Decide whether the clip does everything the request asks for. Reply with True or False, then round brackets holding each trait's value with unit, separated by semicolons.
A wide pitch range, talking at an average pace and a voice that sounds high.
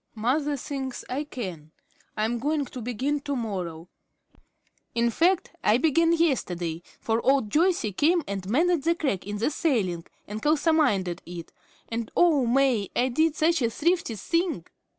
True (6.8 semitones; 150 wpm; 260 Hz)